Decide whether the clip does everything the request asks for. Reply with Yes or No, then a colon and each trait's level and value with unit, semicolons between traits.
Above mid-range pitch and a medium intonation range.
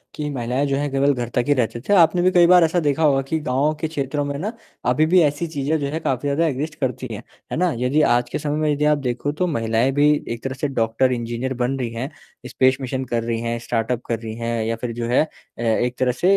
No: low, 135 Hz; average, 3.7 semitones